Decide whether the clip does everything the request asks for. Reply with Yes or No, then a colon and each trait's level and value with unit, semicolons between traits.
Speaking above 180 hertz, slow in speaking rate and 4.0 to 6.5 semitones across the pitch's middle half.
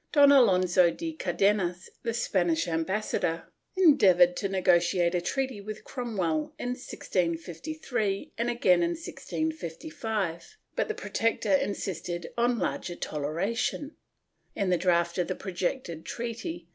Yes: high, 190 Hz; slow, 125 wpm; wide, 5.4 semitones